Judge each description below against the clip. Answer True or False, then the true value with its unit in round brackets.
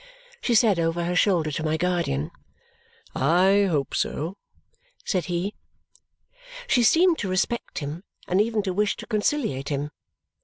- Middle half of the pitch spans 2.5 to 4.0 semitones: False (4.8 semitones)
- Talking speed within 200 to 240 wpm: False (145 wpm)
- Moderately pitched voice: True (180 Hz)